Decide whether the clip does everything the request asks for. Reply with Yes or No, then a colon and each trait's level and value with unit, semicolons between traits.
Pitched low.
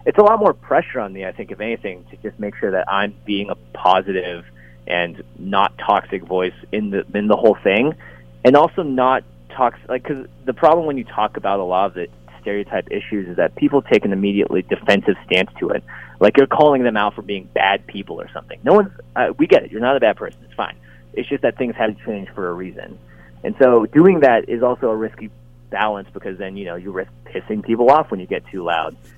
Yes: low, 100 Hz